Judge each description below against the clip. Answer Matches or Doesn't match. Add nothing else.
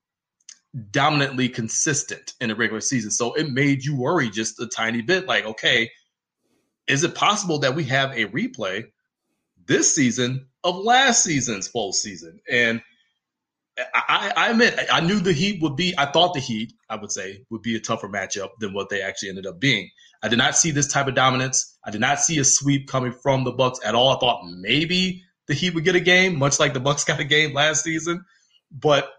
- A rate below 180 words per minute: Doesn't match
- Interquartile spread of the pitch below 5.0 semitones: Doesn't match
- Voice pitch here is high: Doesn't match